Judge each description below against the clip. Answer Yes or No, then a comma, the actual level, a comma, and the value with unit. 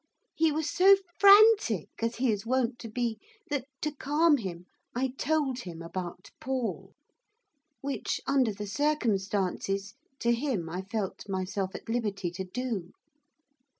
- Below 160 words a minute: Yes, average, 140 wpm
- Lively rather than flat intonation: Yes, wide, 6.1 semitones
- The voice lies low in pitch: No, high, 230 Hz